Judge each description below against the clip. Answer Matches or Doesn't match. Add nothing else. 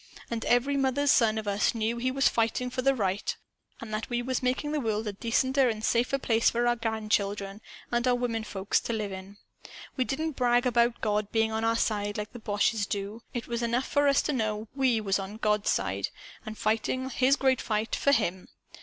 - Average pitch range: Matches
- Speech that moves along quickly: Matches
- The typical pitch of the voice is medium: Doesn't match